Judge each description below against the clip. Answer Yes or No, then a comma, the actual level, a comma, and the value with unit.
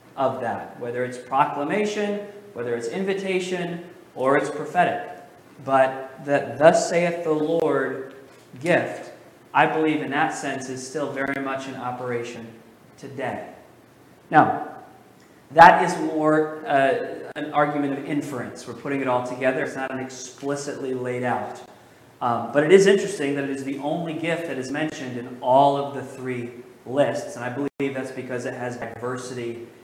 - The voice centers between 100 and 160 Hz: Yes, low, 135 Hz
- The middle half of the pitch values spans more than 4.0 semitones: No, average, 3.6 semitones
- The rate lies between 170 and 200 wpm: No, average, 155 wpm